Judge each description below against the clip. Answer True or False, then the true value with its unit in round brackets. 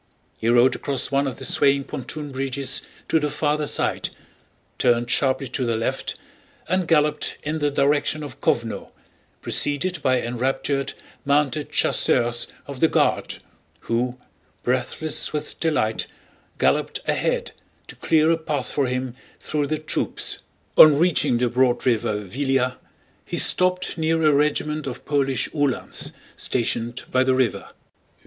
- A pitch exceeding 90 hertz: True (140 Hz)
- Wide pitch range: False (3.2 semitones)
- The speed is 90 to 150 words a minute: True (140 wpm)